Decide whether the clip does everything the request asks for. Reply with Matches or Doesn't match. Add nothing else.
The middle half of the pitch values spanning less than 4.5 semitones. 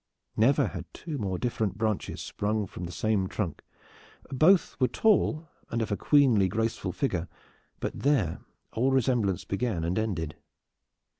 Doesn't match